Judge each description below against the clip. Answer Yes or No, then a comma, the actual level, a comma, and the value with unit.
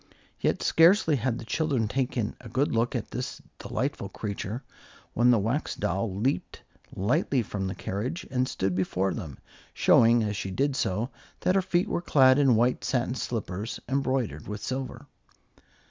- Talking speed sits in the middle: Yes, average, 160 wpm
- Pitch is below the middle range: Yes, low, 120 Hz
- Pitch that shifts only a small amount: No, average, 4.6 semitones